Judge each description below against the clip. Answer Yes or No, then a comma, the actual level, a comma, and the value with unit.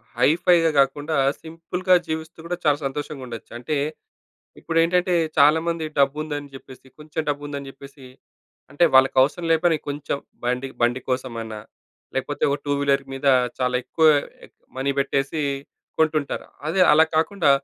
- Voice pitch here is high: No, medium, 145 Hz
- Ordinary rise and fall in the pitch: Yes, average, 3.0 semitones